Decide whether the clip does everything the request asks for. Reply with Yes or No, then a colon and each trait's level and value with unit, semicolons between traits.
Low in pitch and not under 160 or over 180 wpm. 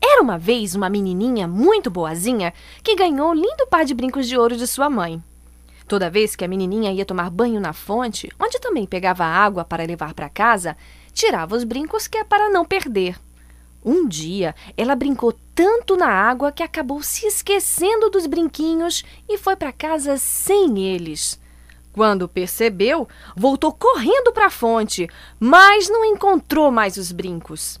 No: high, 235 Hz; average, 165 wpm